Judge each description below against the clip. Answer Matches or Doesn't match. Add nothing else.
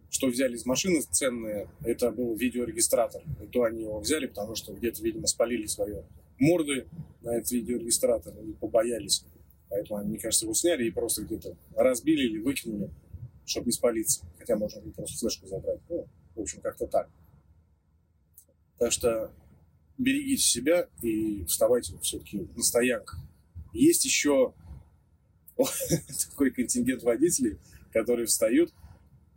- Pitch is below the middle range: Matches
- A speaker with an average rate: Matches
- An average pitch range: Doesn't match